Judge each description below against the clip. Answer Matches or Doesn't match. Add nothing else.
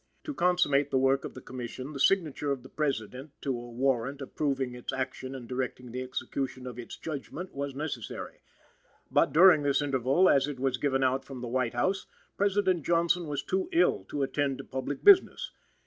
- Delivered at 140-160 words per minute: Doesn't match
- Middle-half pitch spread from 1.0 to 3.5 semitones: Matches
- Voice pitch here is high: Doesn't match